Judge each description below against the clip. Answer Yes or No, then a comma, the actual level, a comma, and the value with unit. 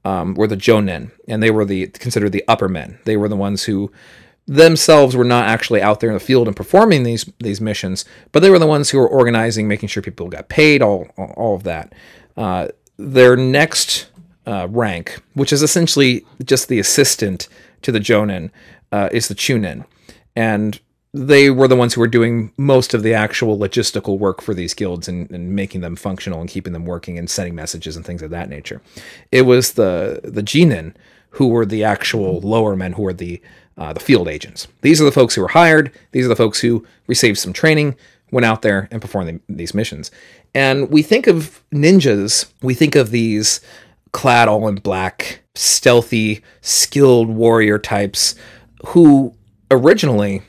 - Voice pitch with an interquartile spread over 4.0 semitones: Yes, average, 4.6 semitones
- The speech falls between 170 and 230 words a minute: Yes, average, 190 wpm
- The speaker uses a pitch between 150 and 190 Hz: No, low, 110 Hz